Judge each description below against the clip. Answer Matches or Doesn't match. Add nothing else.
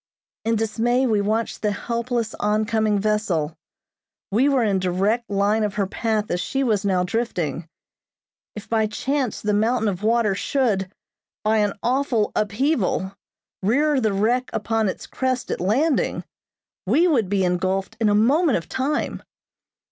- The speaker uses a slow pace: Doesn't match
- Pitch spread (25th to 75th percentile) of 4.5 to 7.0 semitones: Doesn't match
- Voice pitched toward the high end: Matches